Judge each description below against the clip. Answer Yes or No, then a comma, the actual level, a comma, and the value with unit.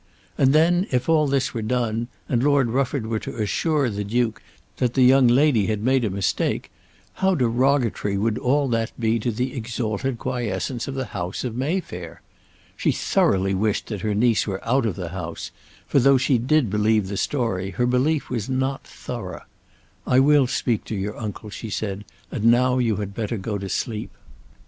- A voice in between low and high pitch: No, low, 120 Hz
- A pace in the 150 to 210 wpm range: Yes, average, 185 wpm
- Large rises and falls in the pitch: No, average, 3.9 semitones